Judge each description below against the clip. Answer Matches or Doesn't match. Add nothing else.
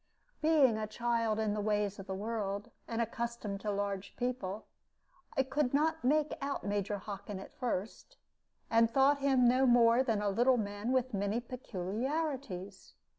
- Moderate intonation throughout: Matches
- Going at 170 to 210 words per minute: Doesn't match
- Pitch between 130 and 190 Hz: Doesn't match